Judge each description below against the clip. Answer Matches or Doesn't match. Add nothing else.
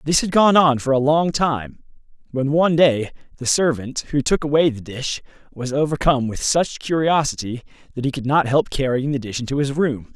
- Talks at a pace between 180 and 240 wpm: Matches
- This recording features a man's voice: Matches